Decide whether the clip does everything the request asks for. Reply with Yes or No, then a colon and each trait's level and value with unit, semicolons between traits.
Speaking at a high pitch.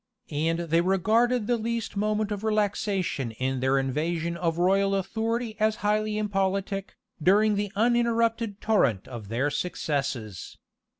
Yes: high, 195 Hz